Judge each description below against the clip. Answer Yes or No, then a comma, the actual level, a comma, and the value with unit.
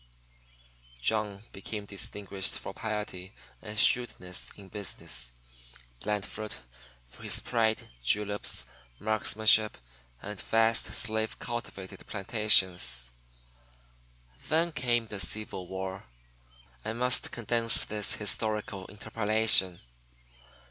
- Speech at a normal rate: No, slow, 95 wpm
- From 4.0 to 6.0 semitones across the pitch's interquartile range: No, narrow, 2.5 semitones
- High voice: No, low, 105 Hz